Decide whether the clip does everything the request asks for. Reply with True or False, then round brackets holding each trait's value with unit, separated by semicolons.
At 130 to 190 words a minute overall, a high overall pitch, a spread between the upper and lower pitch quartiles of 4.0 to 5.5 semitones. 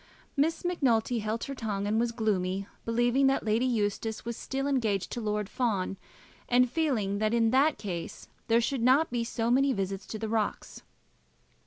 False (175 wpm; 230 Hz; 3.4 semitones)